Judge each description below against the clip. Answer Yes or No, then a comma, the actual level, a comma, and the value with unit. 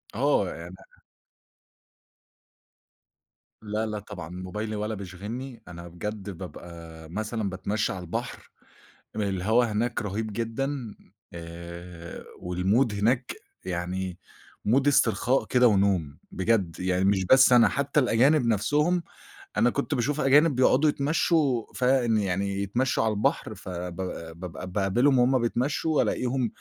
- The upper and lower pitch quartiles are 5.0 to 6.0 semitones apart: Yes, average, 5.3 semitones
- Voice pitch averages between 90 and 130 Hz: Yes, low, 105 Hz